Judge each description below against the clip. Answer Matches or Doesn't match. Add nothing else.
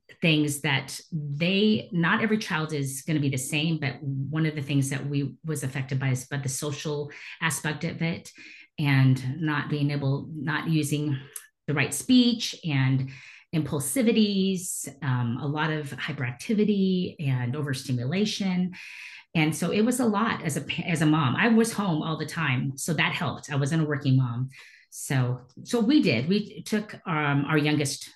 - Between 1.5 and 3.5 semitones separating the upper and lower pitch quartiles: Doesn't match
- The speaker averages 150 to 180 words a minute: Matches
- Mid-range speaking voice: Matches